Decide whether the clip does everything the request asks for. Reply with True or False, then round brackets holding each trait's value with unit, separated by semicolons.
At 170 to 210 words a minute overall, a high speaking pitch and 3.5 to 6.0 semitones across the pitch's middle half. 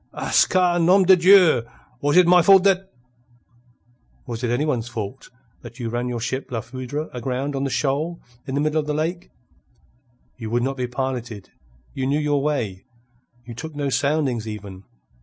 False (185 wpm; 135 Hz; 4.6 semitones)